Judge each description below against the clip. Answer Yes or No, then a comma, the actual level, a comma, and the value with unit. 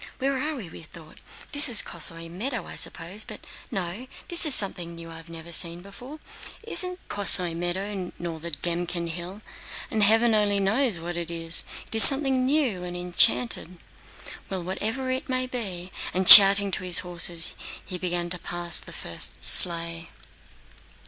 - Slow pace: No, average, 170 wpm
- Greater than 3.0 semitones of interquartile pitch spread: Yes, average, 4.6 semitones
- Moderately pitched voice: Yes, medium, 180 Hz